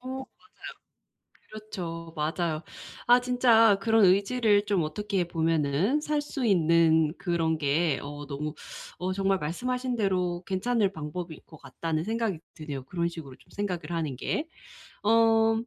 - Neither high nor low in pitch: Yes, medium, 180 Hz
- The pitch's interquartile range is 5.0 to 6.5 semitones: Yes, wide, 5.6 semitones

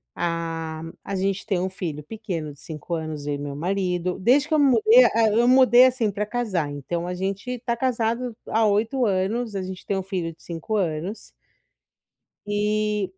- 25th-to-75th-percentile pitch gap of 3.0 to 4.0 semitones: No, average, 5.1 semitones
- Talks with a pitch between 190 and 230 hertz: Yes, high, 195 Hz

